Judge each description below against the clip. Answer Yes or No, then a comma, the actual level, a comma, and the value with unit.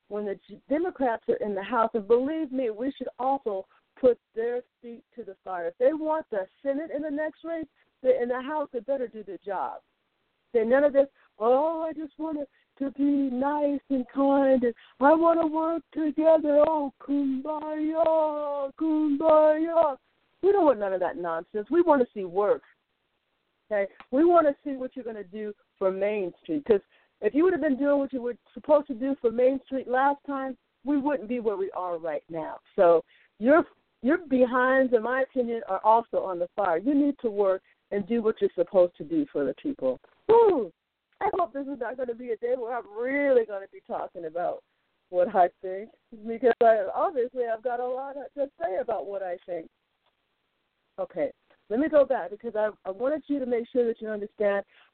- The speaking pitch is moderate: No, very high, 265 Hz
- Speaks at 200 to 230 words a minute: Yes, fast, 205 wpm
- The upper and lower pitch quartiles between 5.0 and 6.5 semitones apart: Yes, wide, 5.4 semitones